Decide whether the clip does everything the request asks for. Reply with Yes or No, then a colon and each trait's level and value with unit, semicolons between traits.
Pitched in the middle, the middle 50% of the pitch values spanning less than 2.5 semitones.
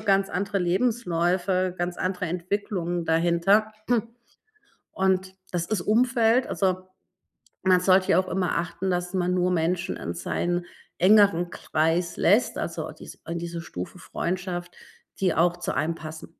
Yes: medium, 180 Hz; narrow, 1.9 semitones